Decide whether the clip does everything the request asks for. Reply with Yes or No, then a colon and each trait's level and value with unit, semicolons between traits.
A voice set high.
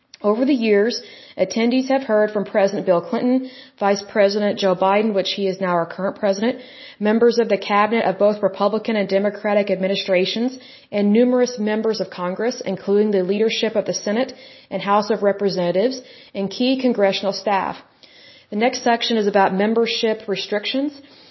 Yes: high, 210 Hz